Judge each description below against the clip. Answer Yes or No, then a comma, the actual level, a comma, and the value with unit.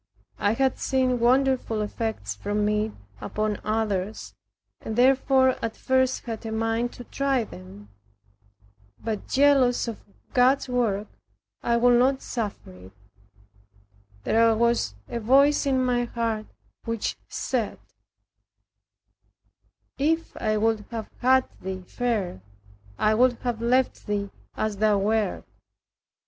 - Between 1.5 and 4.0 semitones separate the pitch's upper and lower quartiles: Yes, average, 3.1 semitones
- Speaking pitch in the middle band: No, high, 230 Hz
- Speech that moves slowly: Yes, slow, 120 wpm